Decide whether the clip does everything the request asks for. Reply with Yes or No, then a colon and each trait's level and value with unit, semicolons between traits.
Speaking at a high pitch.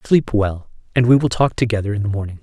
No: low, 110 Hz